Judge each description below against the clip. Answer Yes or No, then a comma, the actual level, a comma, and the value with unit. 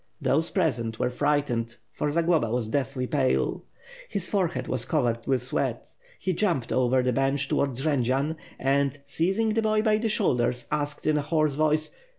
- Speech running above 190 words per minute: No, average, 165 wpm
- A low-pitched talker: No, medium, 145 Hz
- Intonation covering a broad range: No, average, 4.4 semitones